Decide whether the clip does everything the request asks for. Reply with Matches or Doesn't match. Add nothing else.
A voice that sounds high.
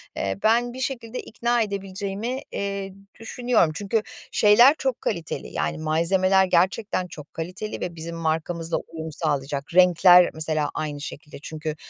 Doesn't match